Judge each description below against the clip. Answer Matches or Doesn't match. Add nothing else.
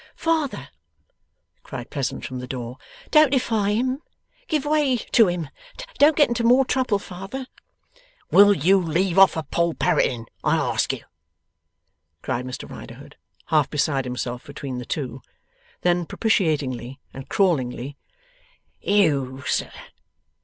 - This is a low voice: Doesn't match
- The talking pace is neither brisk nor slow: Doesn't match